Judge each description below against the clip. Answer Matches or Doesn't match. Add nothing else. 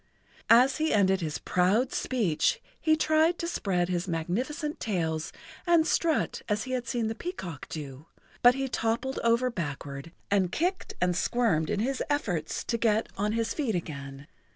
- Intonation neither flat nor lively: Doesn't match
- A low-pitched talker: Doesn't match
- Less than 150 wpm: Doesn't match